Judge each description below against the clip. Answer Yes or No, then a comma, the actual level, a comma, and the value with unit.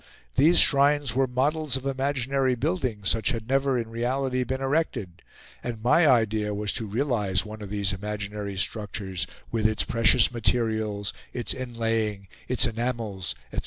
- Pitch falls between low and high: No, low, 115 Hz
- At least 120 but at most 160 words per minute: Yes, average, 155 wpm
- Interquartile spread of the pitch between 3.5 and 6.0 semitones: Yes, average, 4.0 semitones